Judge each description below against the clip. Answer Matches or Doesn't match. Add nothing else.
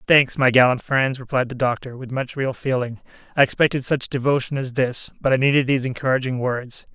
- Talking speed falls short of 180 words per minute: Doesn't match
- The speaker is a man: Matches